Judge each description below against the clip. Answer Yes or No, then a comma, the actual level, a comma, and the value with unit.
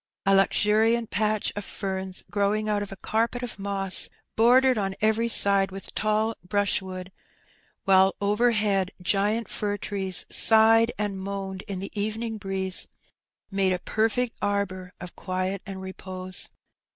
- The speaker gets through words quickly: No, average, 140 wpm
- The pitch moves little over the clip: Yes, narrow, 2.2 semitones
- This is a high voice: Yes, high, 200 Hz